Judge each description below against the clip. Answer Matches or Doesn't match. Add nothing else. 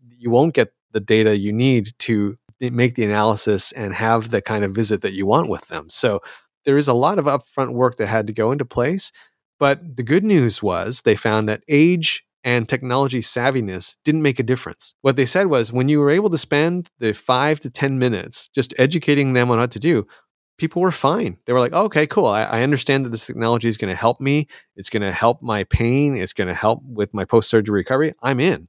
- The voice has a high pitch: Doesn't match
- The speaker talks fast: Matches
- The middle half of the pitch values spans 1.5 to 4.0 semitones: Doesn't match